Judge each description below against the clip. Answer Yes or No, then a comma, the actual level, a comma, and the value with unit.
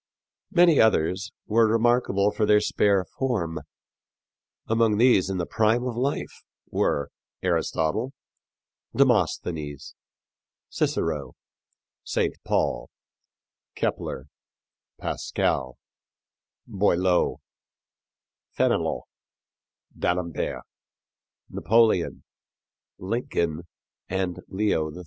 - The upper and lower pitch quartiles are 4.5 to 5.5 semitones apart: Yes, average, 4.9 semitones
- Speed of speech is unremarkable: No, slow, 75 wpm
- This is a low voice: Yes, low, 100 Hz